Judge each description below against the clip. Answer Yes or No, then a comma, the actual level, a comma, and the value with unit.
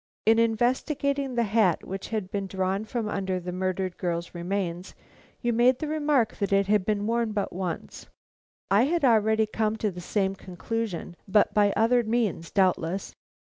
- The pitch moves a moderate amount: Yes, average, 3.5 semitones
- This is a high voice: Yes, high, 210 Hz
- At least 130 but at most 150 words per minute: No, average, 170 wpm